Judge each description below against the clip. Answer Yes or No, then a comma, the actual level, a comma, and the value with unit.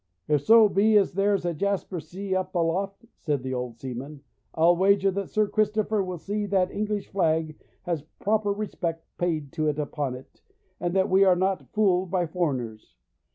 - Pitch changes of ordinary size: Yes, average, 4.3 semitones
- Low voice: No, medium, 180 Hz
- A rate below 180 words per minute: No, average, 185 wpm